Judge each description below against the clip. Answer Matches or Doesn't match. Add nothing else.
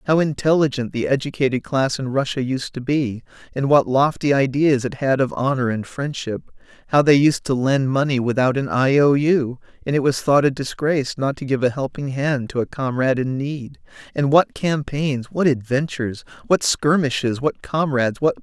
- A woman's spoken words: Doesn't match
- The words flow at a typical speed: Matches